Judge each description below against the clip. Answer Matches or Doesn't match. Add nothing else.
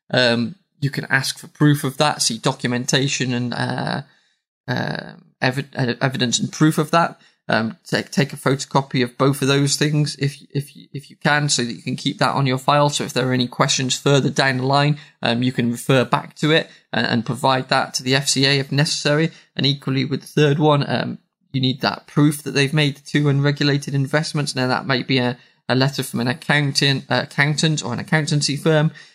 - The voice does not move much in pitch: Matches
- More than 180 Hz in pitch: Doesn't match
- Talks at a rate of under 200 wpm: Doesn't match